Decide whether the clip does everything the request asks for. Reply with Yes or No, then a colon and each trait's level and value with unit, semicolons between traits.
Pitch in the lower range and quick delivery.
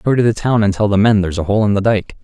Yes: low, 105 Hz; fast, 375 wpm